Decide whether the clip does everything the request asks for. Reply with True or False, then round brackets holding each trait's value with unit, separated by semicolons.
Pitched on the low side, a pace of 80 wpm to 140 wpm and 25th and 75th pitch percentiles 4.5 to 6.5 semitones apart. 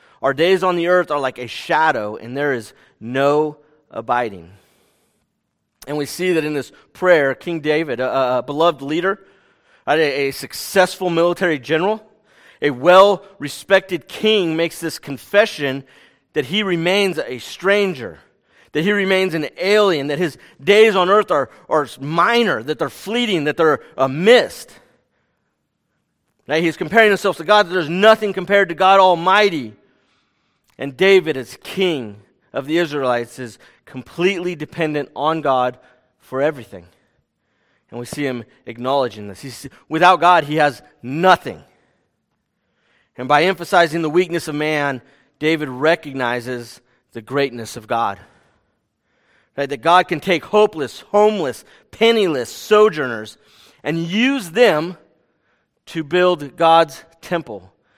False (160 Hz; 135 wpm; 5.2 semitones)